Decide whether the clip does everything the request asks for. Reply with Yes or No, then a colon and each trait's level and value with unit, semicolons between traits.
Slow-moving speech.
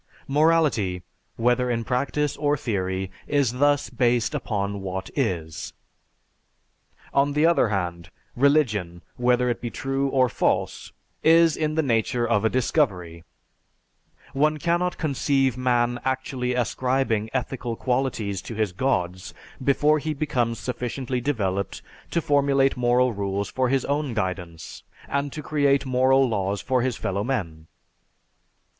Yes: slow, 130 wpm